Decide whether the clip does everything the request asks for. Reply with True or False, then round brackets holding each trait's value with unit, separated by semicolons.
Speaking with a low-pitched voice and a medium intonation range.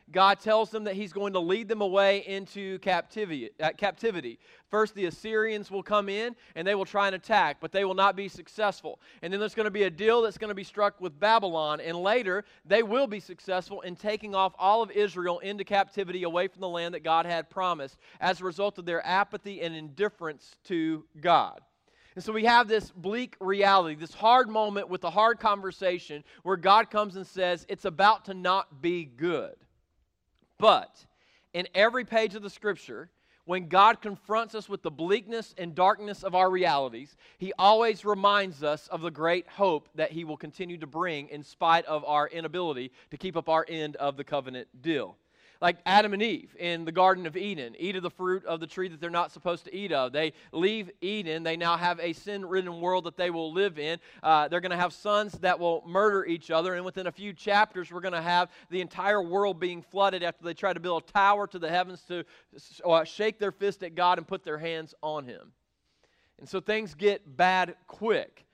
False (185 Hz; 3.3 semitones)